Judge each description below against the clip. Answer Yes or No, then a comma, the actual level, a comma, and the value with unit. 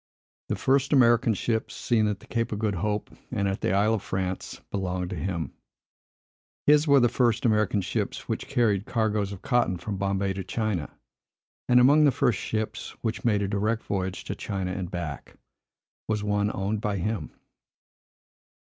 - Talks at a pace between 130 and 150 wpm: No, average, 175 wpm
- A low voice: Yes, low, 105 Hz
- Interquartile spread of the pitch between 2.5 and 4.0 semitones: Yes, average, 3.3 semitones